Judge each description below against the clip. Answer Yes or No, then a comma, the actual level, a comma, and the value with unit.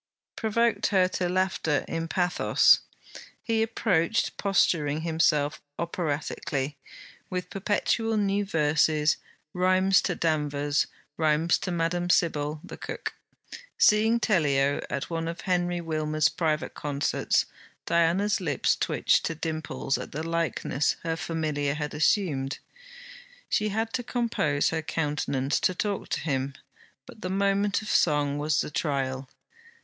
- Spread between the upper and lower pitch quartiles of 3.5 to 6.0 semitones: Yes, average, 4.1 semitones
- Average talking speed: No, slow, 125 wpm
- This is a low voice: No, medium, 165 Hz